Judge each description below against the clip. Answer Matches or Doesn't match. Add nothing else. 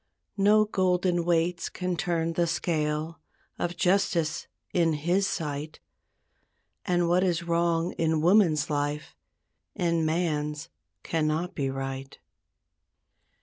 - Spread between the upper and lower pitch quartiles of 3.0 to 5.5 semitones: Doesn't match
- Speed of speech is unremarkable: Doesn't match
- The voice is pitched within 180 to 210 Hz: Doesn't match